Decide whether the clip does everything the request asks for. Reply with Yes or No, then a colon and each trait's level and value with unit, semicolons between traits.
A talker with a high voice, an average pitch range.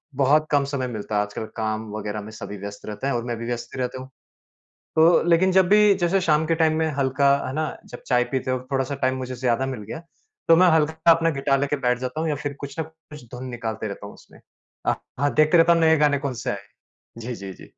No: low, 135 Hz; average, 5.0 semitones